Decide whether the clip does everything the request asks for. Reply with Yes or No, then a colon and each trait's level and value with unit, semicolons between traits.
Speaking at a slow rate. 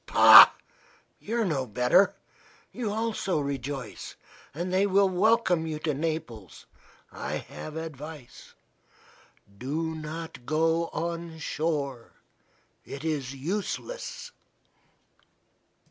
Yes: slow, 100 wpm